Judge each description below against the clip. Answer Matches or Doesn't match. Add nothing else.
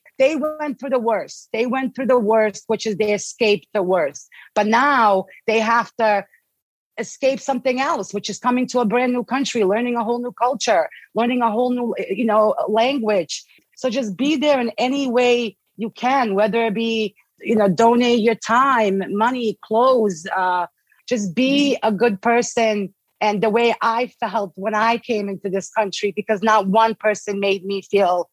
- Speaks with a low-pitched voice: Doesn't match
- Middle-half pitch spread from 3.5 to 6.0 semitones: Doesn't match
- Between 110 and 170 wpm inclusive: Doesn't match